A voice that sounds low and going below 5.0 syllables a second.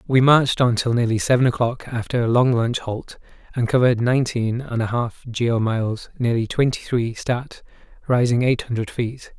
No: low, 120 Hz; 5.4 syllables/s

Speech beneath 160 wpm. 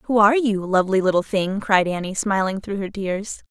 No: fast, 205 wpm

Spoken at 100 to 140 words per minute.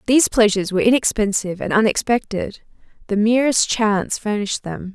Yes: slow, 135 wpm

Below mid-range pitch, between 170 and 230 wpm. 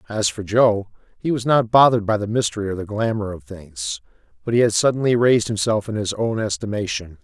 Yes: low, 110 Hz; fast, 205 wpm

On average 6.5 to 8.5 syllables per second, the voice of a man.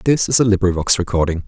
Yes: 6.8 syllables/s; male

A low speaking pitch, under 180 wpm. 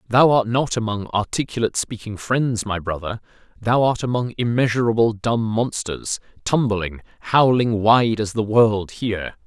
Yes: low, 115 Hz; average, 140 wpm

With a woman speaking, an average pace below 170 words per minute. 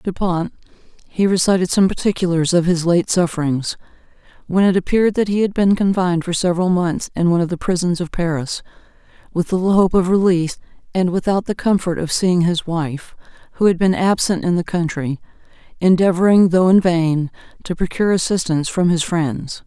No: female; average, 175 wpm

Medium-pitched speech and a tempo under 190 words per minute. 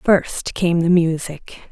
Yes: medium, 170 Hz; average, 140 wpm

